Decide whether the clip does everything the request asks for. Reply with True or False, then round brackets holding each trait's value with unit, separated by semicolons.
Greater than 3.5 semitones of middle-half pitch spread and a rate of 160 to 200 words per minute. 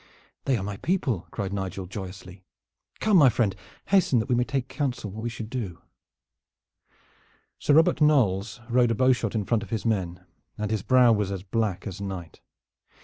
True (4.6 semitones; 180 wpm)